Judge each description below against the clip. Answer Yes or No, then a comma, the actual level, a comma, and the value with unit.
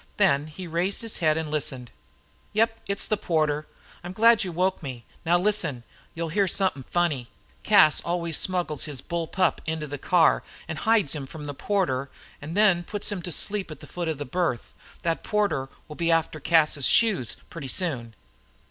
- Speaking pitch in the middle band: Yes, medium, 165 Hz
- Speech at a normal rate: Yes, average, 190 wpm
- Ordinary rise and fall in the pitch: Yes, average, 4.3 semitones